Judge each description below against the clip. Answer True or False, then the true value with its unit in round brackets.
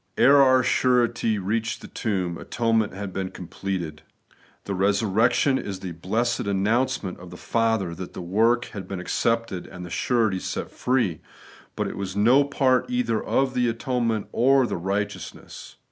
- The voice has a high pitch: False (110 Hz)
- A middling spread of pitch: True (4.4 semitones)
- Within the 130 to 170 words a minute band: True (160 wpm)